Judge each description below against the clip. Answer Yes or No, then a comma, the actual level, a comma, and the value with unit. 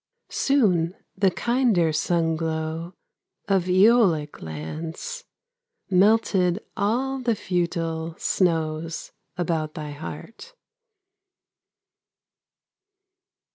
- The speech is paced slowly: Yes, slow, 65 wpm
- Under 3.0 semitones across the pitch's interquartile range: No, average, 4.7 semitones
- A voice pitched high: No, medium, 175 Hz